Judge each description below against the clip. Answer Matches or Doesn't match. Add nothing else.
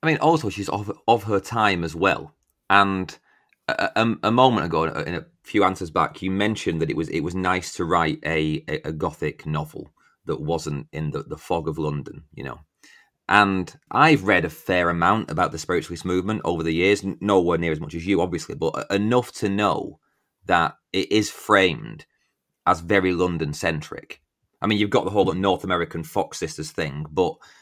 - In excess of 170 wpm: Matches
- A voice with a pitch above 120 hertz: Doesn't match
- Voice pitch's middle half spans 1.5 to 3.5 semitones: Doesn't match